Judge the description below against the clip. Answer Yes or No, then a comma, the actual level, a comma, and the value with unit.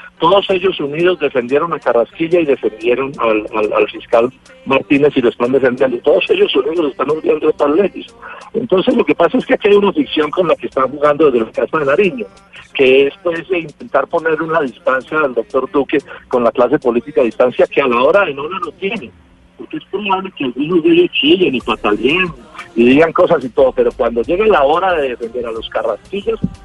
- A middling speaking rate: No, fast, 215 wpm